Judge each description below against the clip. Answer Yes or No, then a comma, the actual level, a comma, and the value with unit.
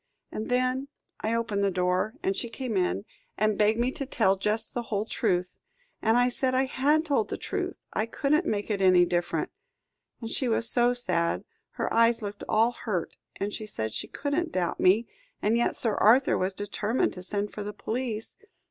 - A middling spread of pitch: Yes, average, 3.6 semitones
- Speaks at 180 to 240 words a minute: Yes, average, 195 wpm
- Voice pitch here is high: Yes, high, 220 Hz